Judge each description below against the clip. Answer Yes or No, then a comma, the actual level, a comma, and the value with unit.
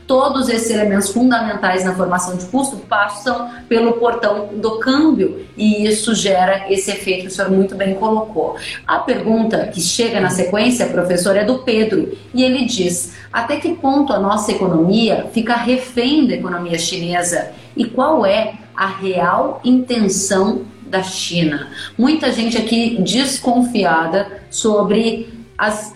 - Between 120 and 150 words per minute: Yes, average, 145 wpm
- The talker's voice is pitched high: Yes, high, 215 Hz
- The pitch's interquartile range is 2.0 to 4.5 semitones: Yes, average, 4.0 semitones